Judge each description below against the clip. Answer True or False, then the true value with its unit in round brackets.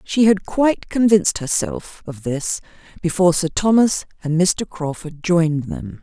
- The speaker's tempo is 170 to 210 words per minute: False (150 wpm)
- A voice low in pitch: False (170 Hz)